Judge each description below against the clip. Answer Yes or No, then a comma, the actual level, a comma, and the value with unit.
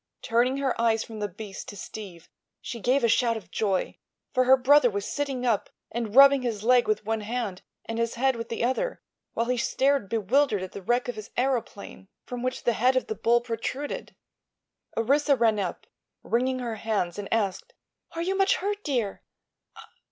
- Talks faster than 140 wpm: Yes, average, 190 wpm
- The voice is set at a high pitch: Yes, high, 235 Hz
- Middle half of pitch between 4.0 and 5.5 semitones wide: No, average, 3.4 semitones